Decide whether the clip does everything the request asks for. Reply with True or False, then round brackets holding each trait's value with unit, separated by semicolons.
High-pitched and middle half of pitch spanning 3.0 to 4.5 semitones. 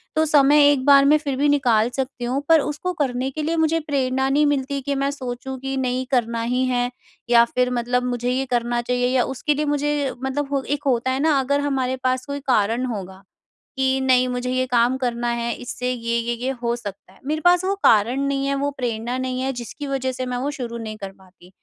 False (255 Hz; 2.6 semitones)